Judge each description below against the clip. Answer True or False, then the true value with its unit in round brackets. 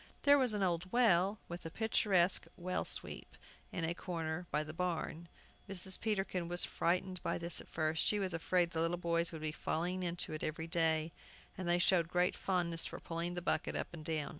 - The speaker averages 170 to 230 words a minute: True (200 wpm)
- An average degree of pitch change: False (1.9 semitones)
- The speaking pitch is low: False (175 Hz)